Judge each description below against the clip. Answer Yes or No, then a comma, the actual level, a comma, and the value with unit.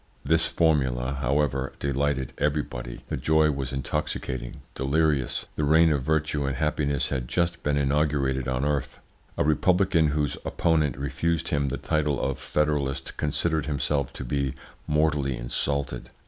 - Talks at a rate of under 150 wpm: Yes, average, 140 wpm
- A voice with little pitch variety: Yes, narrow, 2.3 semitones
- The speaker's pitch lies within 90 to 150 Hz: No, very low, 70 Hz